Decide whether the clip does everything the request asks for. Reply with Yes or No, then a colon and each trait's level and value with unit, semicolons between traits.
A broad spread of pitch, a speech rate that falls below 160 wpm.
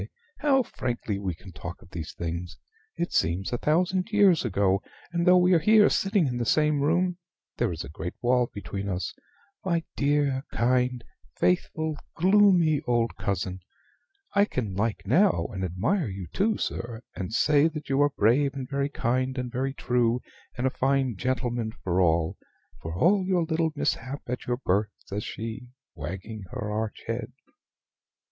No: wide, 7.6 semitones; average, 165 wpm